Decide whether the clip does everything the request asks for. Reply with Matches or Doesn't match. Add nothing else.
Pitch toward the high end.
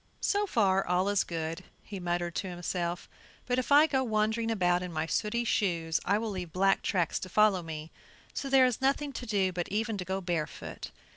Matches